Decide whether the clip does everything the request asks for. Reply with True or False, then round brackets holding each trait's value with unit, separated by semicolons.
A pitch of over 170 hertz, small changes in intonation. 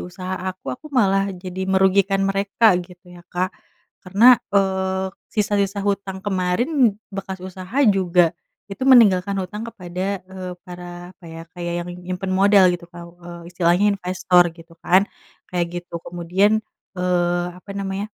True (185 Hz; 1.6 semitones)